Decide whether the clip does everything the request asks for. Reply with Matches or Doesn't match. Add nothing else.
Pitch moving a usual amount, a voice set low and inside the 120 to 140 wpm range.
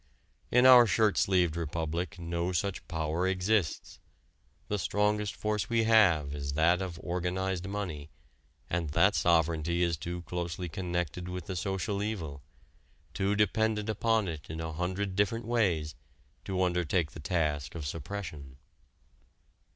Matches